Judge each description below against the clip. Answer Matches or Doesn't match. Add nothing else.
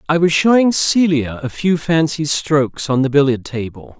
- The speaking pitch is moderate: Matches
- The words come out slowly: Doesn't match